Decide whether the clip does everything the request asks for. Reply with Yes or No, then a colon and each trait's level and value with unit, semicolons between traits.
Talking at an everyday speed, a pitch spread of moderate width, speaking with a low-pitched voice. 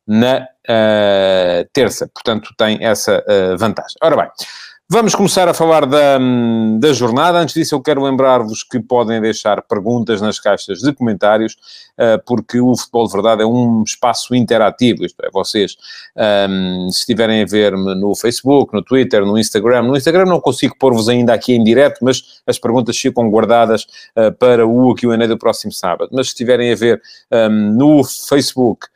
Yes: average, 170 wpm; average, 3.1 semitones; low, 120 Hz